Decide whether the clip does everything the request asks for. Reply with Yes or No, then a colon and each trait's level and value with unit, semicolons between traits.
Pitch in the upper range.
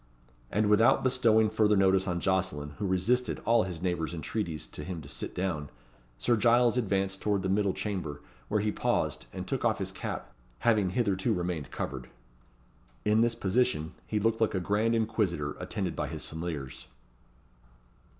No: very low, 95 Hz